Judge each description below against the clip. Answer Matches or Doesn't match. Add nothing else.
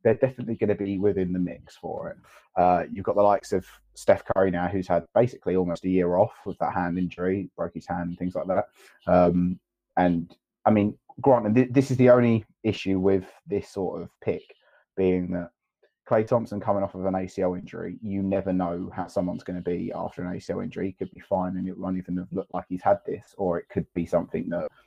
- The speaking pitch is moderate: Doesn't match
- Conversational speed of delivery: Doesn't match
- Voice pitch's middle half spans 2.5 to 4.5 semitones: Doesn't match